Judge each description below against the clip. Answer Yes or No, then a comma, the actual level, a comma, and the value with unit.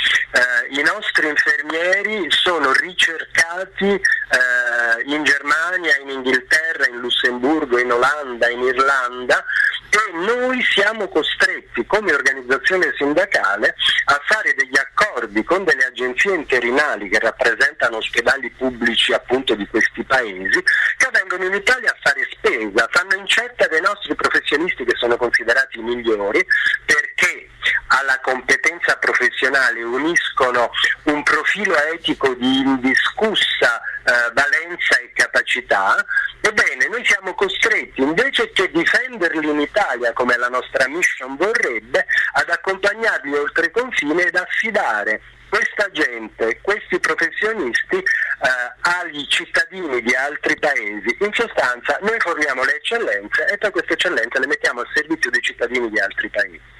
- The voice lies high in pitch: Yes, high, 210 Hz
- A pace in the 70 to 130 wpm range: Yes, average, 125 wpm